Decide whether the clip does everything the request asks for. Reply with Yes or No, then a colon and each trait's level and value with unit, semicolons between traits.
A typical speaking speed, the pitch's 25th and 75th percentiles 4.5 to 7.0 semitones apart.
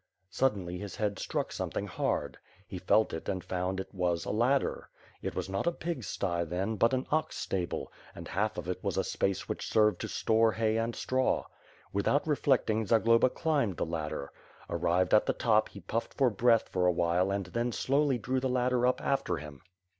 Yes: average, 195 wpm; average, 5.3 semitones